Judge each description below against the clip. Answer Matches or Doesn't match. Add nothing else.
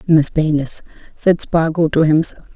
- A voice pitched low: Doesn't match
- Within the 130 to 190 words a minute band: Matches